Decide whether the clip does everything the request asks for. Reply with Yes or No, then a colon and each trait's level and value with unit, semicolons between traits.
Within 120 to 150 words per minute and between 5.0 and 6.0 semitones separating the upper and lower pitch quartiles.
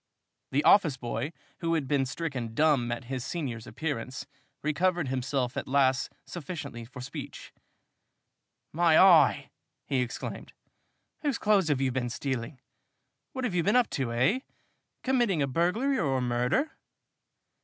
Yes: average, 145 wpm; average, 5.3 semitones